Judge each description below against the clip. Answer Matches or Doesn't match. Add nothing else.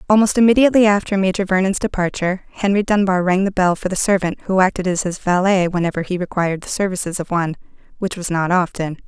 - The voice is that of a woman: Matches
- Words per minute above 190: Matches